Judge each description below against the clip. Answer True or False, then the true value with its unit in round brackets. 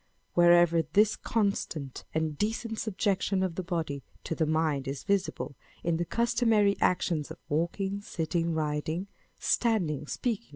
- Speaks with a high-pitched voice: False (175 Hz)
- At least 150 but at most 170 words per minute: False (135 wpm)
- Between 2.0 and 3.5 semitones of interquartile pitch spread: False (4.4 semitones)